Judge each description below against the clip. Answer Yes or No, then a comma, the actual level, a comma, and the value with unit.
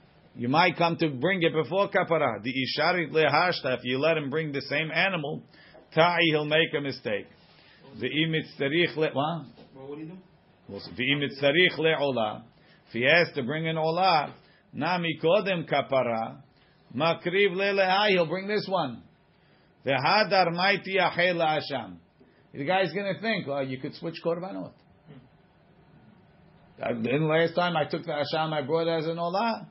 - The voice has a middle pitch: Yes, medium, 160 Hz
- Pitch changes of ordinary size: Yes, average, 3.9 semitones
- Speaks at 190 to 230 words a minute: No, average, 150 wpm